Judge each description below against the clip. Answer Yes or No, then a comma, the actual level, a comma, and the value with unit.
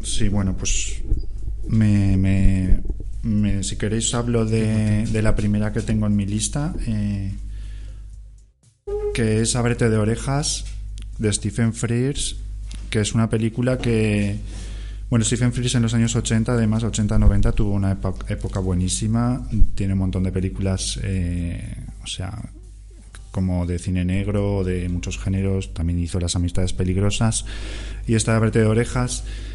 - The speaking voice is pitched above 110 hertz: No, low, 105 Hz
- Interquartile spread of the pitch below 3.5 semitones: Yes, narrow, 2.6 semitones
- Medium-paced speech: Yes, average, 145 wpm